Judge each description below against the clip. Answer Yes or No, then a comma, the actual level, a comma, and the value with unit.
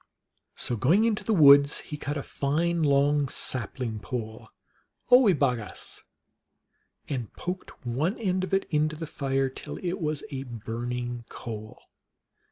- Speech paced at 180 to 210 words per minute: No, average, 150 wpm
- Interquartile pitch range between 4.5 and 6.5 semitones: Yes, wide, 5.4 semitones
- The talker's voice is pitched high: No, medium, 140 Hz